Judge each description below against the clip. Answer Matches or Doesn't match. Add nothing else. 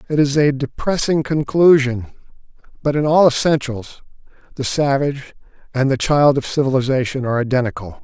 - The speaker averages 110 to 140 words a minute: Matches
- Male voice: Matches